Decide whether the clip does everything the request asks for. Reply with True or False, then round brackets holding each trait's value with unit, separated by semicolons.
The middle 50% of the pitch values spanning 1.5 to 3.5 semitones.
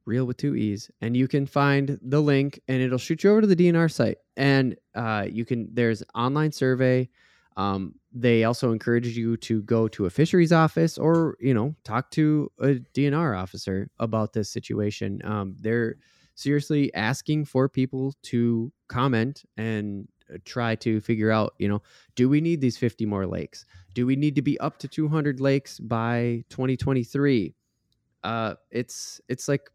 False (4.0 semitones)